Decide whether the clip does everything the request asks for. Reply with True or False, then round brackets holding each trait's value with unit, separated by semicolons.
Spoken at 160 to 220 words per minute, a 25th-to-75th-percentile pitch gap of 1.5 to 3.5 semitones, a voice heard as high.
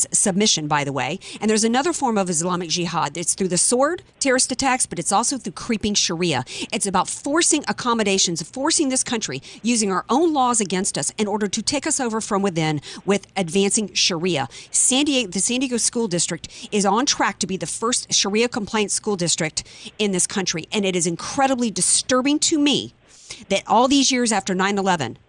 False (190 wpm; 5.4 semitones; 205 Hz)